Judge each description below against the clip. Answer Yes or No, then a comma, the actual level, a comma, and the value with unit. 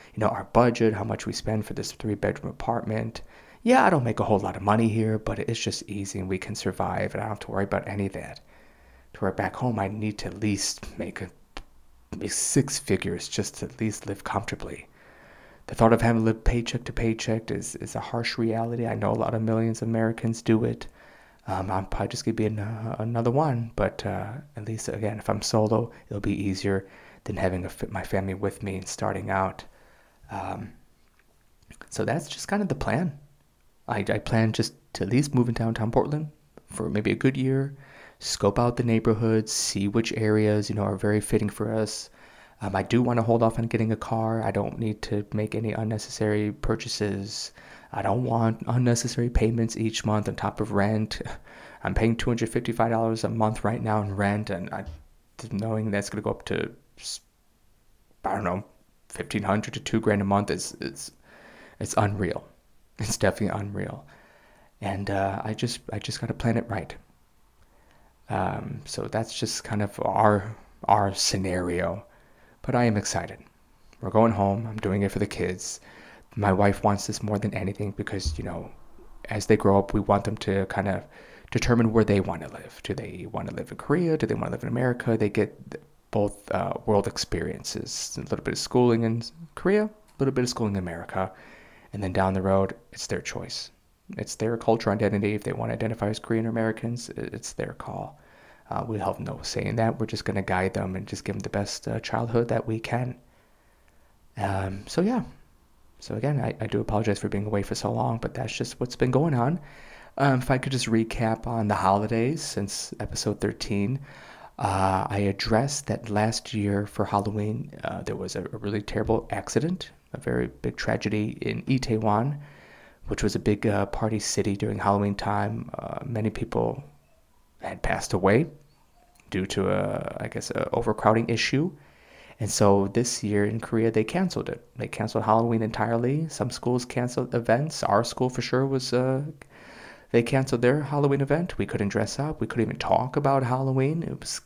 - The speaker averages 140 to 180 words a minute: No, average, 200 wpm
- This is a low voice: Yes, low, 110 Hz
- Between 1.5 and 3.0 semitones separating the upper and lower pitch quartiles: Yes, narrow, 2.6 semitones